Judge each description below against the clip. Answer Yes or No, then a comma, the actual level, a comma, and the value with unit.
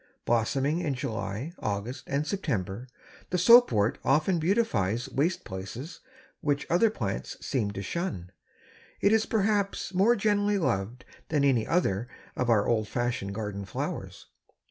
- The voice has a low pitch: Yes, low, 130 Hz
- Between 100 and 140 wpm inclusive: Yes, slow, 135 wpm